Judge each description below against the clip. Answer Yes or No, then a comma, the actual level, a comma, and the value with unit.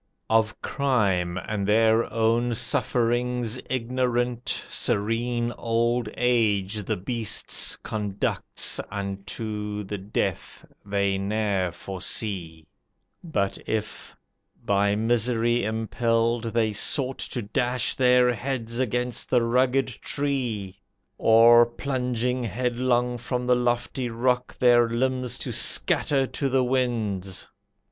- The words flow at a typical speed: No, slow, 105 wpm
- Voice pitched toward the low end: Yes, low, 115 Hz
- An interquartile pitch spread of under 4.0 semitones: Yes, average, 2.9 semitones